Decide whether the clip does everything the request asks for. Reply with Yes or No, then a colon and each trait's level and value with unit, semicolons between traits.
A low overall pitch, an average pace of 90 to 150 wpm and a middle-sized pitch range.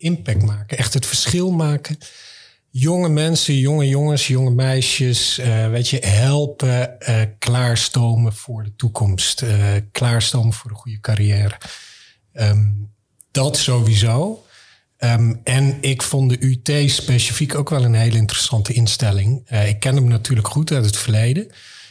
Yes: low, 125 Hz; average, 140 wpm; average, 3.6 semitones